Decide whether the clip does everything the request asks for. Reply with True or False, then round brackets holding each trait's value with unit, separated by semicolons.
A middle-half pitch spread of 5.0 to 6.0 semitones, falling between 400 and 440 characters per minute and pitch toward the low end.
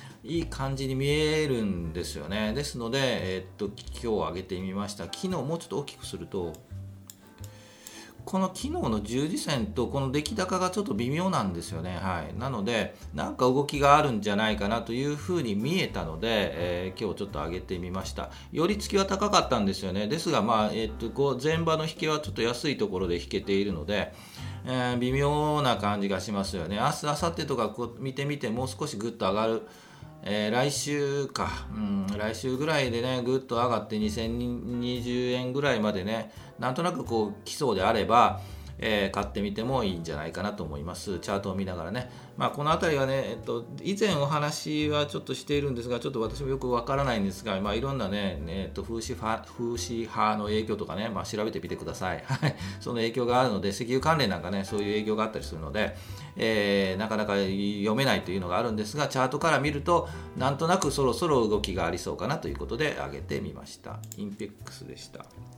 True (5.5 semitones; 415 characters per minute; 110 Hz)